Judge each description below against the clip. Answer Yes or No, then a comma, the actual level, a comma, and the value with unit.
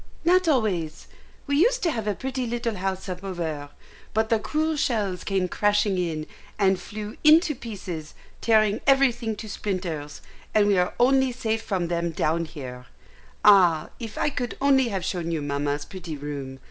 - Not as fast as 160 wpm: No, average, 170 wpm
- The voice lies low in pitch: No, high, 200 Hz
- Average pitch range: No, wide, 6.0 semitones